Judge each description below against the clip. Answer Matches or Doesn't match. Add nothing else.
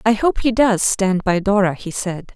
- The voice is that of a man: Doesn't match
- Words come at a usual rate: Doesn't match